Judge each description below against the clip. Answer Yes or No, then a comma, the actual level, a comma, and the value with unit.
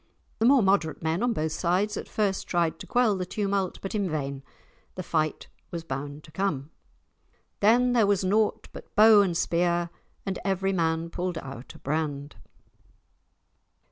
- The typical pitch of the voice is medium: Yes, medium, 180 Hz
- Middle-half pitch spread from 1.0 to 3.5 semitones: No, average, 4.1 semitones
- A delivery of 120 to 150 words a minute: No, average, 165 wpm